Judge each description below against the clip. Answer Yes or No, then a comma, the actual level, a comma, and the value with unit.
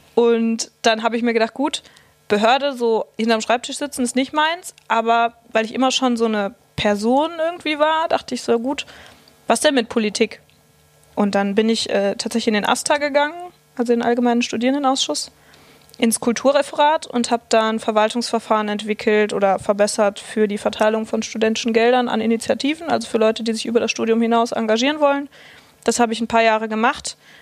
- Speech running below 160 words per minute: No, average, 185 wpm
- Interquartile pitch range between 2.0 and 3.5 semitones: Yes, average, 3.0 semitones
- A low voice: No, high, 230 Hz